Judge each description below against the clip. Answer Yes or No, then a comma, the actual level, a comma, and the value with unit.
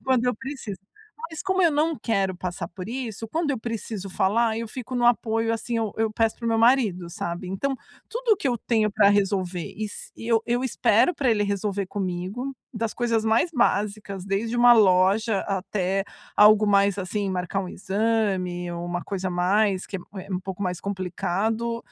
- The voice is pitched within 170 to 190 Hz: No, high, 210 Hz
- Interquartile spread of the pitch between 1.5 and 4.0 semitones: Yes, average, 3.5 semitones